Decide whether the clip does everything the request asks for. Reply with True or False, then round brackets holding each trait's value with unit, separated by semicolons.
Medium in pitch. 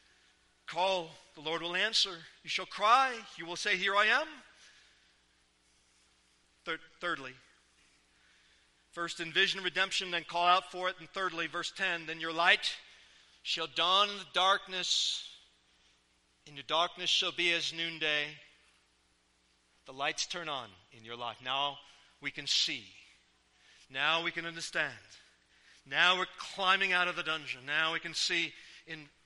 True (160 Hz)